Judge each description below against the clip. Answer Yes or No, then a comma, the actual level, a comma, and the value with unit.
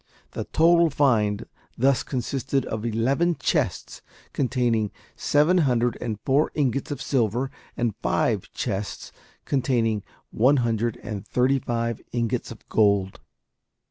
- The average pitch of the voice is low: Yes, low, 120 Hz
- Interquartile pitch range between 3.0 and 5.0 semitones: Yes, average, 3.5 semitones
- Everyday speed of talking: No, slow, 120 wpm